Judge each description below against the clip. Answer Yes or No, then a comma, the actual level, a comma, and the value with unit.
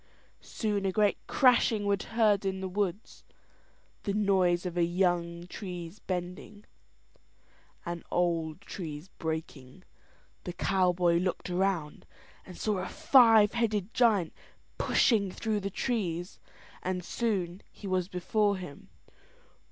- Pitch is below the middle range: No, medium, 185 Hz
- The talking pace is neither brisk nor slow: No, slow, 120 wpm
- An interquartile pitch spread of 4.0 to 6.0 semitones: No, average, 3.0 semitones